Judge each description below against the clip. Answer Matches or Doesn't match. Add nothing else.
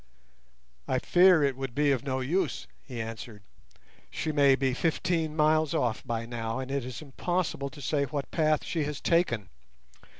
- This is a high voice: Doesn't match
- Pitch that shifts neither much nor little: Matches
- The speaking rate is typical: Matches